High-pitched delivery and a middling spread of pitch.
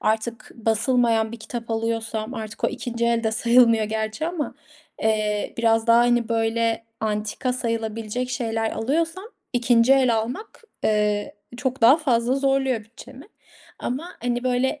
No: high, 230 Hz; narrow, 2.2 semitones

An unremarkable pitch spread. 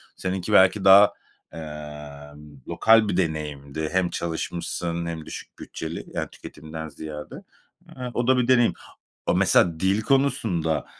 Yes: average, 4.8 semitones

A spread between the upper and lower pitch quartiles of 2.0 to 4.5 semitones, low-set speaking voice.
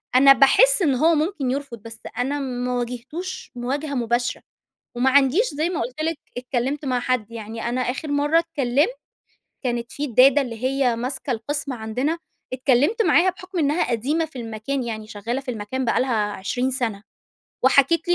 No: average, 3.5 semitones; very high, 260 Hz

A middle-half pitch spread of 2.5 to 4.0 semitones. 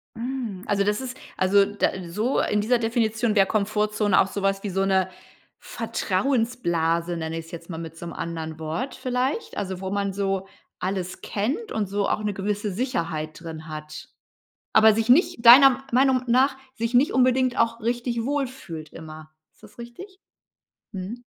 No: average, 5.0 semitones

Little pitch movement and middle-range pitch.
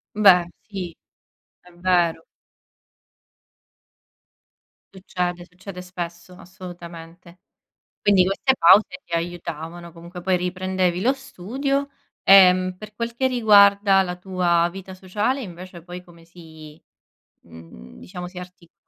Yes: narrow, 1.9 semitones; medium, 180 Hz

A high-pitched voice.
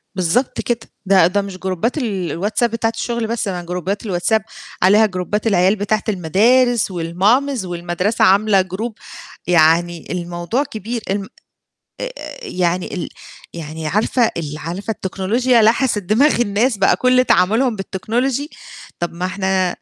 Yes: high, 200 Hz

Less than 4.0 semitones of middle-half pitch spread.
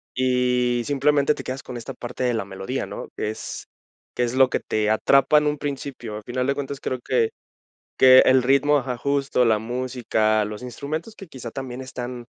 Yes: narrow, 2.4 semitones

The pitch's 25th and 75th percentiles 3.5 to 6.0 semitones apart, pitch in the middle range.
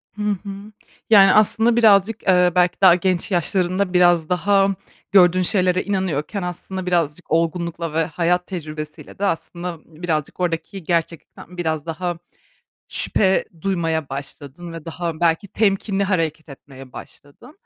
No: average, 3.0 semitones; medium, 175 Hz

